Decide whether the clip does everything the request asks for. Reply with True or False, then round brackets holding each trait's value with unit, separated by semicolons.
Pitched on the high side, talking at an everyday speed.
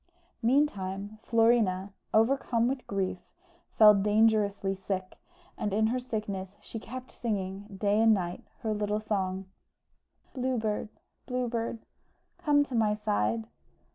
False (215 Hz; 125 wpm)